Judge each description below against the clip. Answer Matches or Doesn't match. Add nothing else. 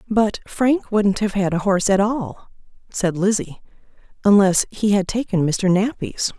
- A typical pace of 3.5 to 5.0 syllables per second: Matches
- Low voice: Doesn't match